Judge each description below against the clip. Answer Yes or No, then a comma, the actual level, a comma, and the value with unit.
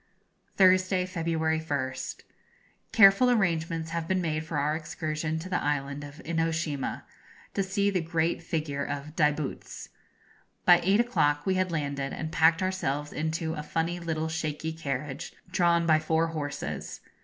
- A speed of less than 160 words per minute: Yes, average, 145 wpm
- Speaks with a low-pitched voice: No, medium, 160 Hz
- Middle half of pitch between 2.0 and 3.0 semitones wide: Yes, narrow, 2.6 semitones